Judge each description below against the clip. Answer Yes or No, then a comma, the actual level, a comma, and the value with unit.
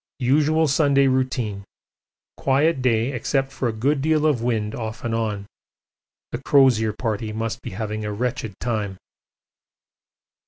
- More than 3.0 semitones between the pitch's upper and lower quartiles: Yes, average, 3.8 semitones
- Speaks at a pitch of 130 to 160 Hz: No, low, 120 Hz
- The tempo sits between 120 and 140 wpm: Yes, slow, 135 wpm